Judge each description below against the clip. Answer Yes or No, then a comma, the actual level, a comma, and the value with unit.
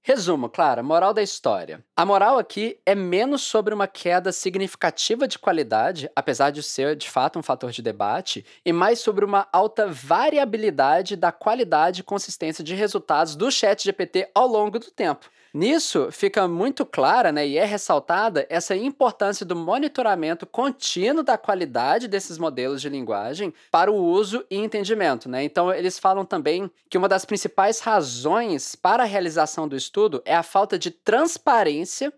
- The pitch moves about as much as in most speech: Yes, average, 4.6 semitones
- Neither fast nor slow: Yes, average, 165 wpm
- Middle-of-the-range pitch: No, high, 200 Hz